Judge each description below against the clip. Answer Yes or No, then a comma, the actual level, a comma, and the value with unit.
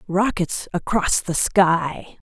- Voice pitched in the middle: Yes, medium, 180 Hz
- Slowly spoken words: Yes, slow, 105 wpm